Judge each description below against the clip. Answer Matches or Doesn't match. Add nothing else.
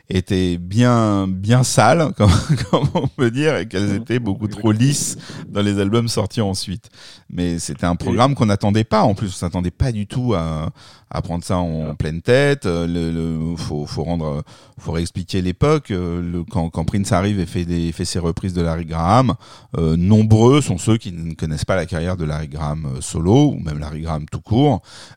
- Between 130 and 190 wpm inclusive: Doesn't match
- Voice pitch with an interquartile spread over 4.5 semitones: Matches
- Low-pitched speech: Matches